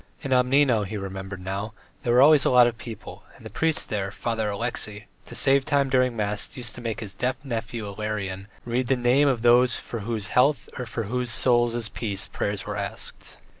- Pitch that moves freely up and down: No, average, 3.3 semitones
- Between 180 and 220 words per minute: Yes, average, 200 wpm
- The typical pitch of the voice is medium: No, low, 115 Hz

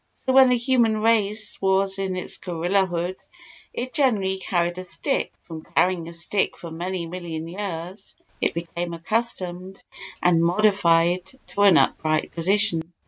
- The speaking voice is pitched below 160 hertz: No, medium, 185 Hz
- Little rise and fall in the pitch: No, average, 3.2 semitones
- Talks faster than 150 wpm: No, average, 145 wpm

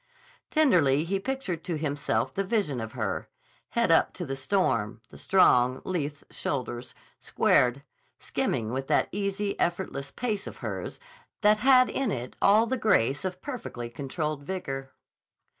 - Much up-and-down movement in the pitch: Yes, wide, 7.2 semitones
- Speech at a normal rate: Yes, average, 145 wpm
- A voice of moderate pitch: Yes, medium, 165 Hz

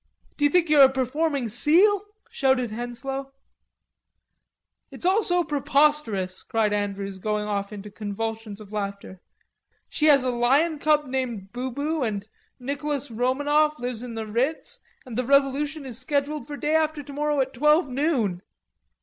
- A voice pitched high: Yes, very high, 265 Hz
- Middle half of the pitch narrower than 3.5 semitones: No, average, 5.1 semitones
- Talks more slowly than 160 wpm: Yes, average, 150 wpm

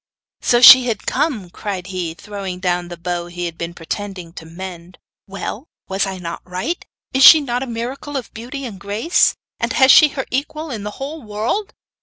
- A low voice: No, high, 205 Hz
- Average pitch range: No, wide, 6.6 semitones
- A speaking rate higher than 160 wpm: Yes, average, 195 wpm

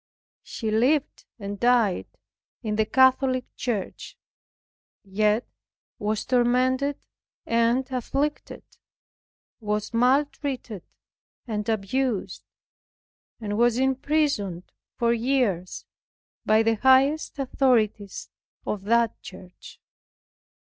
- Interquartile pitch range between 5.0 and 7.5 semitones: No, average, 3.8 semitones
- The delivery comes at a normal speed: No, slow, 85 wpm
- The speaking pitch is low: No, high, 235 Hz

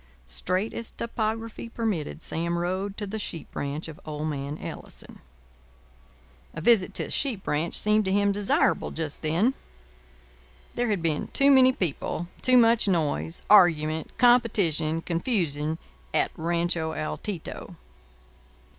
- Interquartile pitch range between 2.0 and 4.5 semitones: No, wide, 5.5 semitones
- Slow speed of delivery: Yes, slow, 130 wpm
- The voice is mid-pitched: Yes, medium, 175 Hz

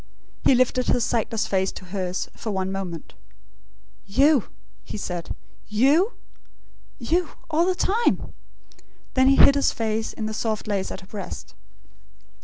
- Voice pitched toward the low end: No, high, 220 Hz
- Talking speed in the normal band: Yes, average, 145 wpm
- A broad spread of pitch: Yes, wide, 6.0 semitones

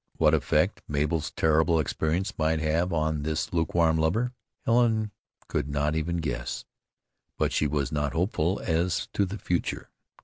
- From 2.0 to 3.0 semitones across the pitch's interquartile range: Yes, narrow, 2.6 semitones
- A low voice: Yes, very low, 80 Hz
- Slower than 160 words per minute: Yes, average, 145 wpm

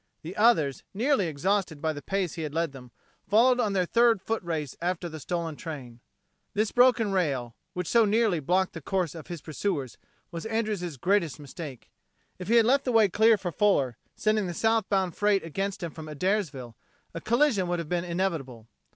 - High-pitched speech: No, medium, 180 Hz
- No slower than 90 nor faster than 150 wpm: No, average, 190 wpm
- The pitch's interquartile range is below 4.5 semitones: No, average, 5.1 semitones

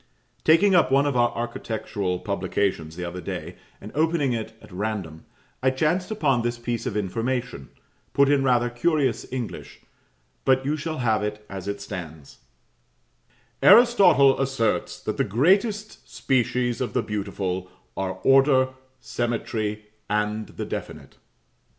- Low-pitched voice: Yes, low, 120 Hz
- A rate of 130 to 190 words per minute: Yes, average, 140 wpm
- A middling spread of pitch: Yes, average, 4.7 semitones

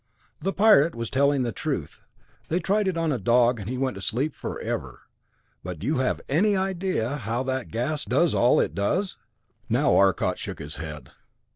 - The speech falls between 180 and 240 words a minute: Yes, average, 185 wpm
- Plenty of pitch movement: Yes, wide, 6.5 semitones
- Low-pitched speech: Yes, low, 130 Hz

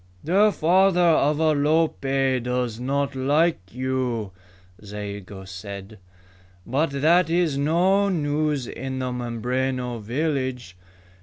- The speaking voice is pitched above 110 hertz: Yes, low, 135 Hz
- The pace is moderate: No, slow, 100 wpm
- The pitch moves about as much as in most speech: Yes, average, 4.5 semitones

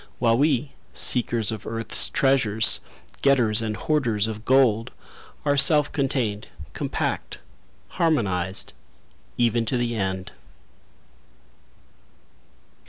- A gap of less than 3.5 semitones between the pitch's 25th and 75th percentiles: No, average, 4.0 semitones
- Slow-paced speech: Yes, slow, 95 wpm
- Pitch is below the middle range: Yes, low, 115 Hz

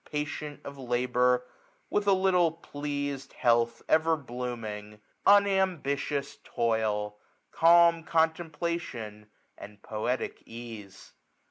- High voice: No, medium, 140 Hz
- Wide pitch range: Yes, wide, 5.9 semitones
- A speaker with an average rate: No, slow, 95 wpm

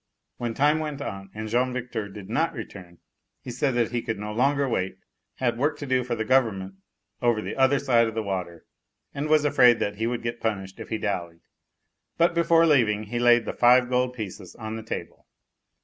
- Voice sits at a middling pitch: No, low, 120 Hz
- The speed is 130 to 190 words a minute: No, fast, 205 wpm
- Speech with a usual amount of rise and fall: Yes, average, 3.5 semitones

